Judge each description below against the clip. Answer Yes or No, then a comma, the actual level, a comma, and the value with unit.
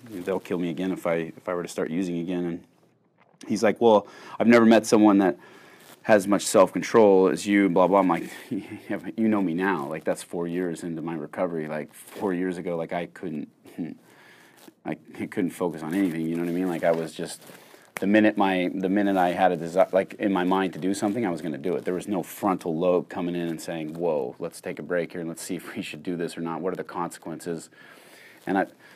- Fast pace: Yes, fast, 245 wpm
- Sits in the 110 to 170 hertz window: No, very low, 90 Hz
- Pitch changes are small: Yes, narrow, 2.3 semitones